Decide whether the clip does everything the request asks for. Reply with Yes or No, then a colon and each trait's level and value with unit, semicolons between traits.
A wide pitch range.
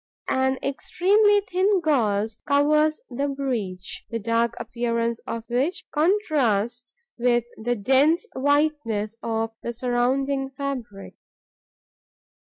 No: average, 4.3 semitones